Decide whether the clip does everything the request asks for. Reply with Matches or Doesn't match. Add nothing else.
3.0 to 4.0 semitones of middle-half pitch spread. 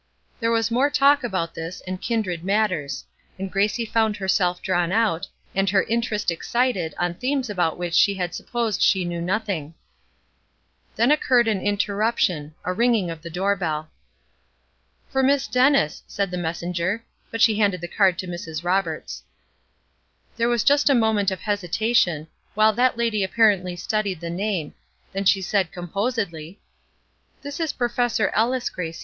Doesn't match